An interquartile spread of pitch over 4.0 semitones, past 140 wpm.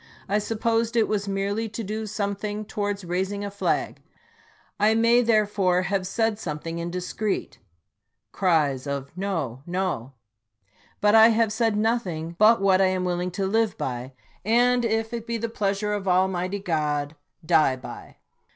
No: average, 3.7 semitones; average, 165 wpm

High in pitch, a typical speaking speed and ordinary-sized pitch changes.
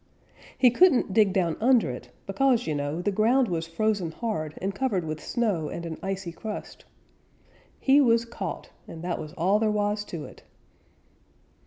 No: high, 200 Hz; average, 170 wpm; wide, 5.7 semitones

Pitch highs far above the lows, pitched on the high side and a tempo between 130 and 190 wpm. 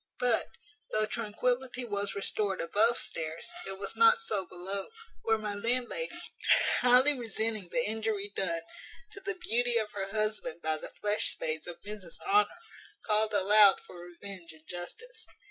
No: average, 3.8 semitones; high, 210 Hz; average, 150 wpm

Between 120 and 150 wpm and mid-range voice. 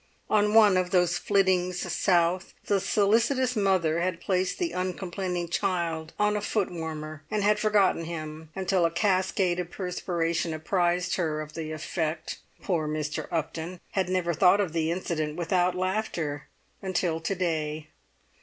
Yes: average, 145 wpm; medium, 180 Hz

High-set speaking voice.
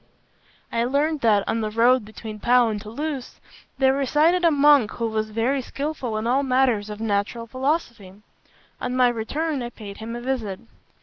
Yes: high, 240 Hz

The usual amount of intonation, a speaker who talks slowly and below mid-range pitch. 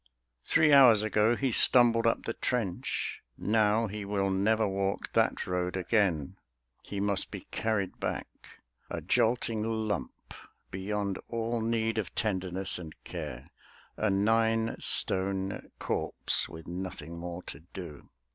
Yes: average, 3.2 semitones; slow, 130 wpm; low, 105 Hz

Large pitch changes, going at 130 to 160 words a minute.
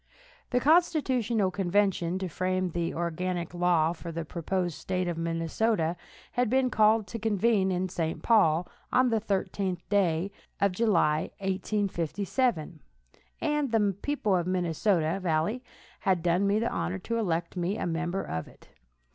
No: average, 4.0 semitones; average, 150 wpm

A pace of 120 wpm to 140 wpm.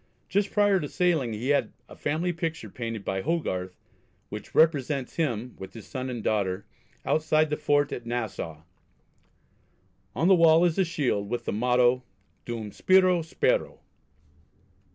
No: average, 150 wpm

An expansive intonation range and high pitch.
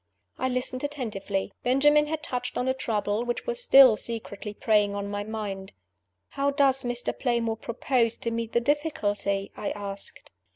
No: average, 4.5 semitones; high, 235 Hz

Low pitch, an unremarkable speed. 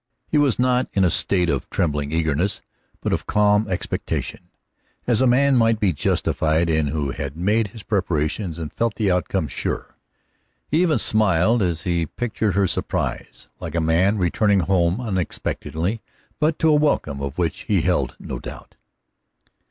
Yes: very low, 95 Hz; average, 165 wpm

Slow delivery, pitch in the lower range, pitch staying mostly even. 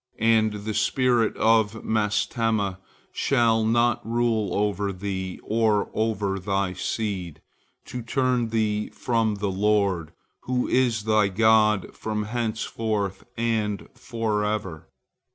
Yes: slow, 110 wpm; low, 110 Hz; narrow, 2.0 semitones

